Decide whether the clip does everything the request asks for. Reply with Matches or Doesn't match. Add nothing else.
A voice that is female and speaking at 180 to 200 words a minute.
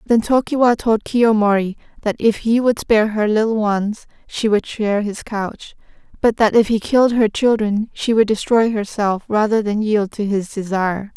Matches